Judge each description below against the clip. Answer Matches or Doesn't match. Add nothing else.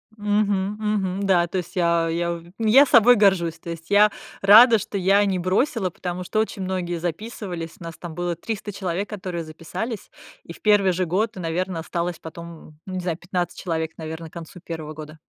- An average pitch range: Matches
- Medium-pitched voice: Matches